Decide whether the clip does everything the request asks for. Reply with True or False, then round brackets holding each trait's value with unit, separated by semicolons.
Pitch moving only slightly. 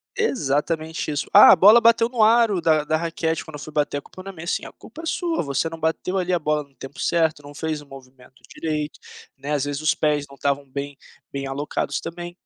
False (3.5 semitones)